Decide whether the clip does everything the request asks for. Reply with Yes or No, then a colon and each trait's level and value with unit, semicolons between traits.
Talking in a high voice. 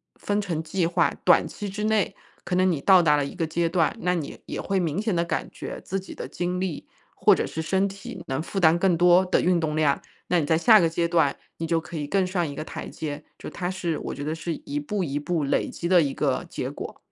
No: medium, 170 Hz